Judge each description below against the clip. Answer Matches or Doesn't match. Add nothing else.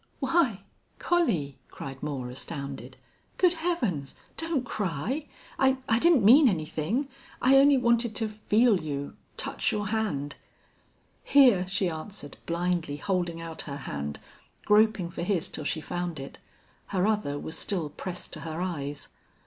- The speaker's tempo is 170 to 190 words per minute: Doesn't match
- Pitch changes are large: Matches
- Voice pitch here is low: Doesn't match